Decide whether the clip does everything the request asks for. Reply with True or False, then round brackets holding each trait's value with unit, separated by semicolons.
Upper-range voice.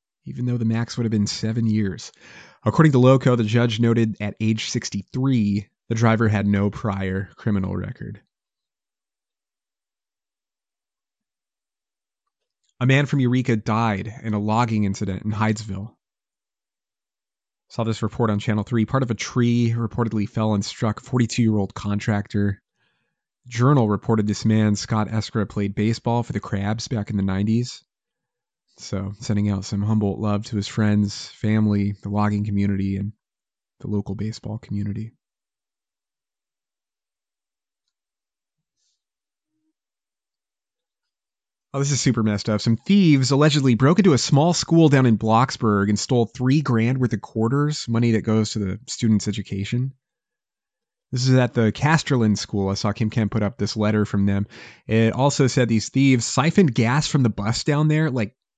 False (110 Hz)